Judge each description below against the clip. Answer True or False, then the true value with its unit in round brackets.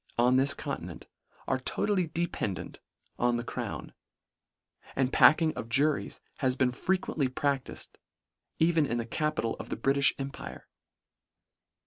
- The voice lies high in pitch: False (135 Hz)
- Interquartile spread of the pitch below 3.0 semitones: False (3.7 semitones)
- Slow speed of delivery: True (125 wpm)